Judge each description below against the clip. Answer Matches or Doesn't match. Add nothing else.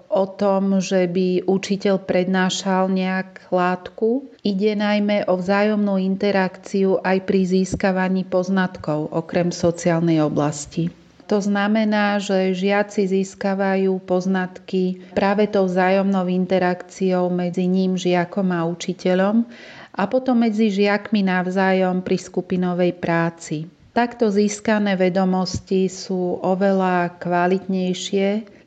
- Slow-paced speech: Matches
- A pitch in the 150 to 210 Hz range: Matches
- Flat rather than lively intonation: Matches